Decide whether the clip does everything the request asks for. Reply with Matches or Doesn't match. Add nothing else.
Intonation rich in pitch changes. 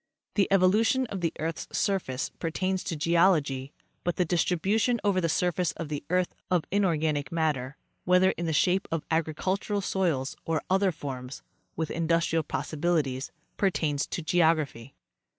Doesn't match